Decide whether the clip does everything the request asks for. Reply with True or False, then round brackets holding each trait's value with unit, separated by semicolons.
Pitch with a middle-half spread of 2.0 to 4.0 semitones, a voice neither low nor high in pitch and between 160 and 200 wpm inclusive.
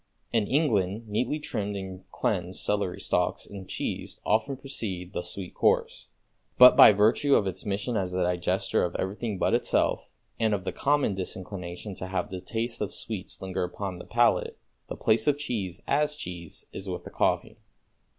False (3.7 semitones; 100 Hz; 175 wpm)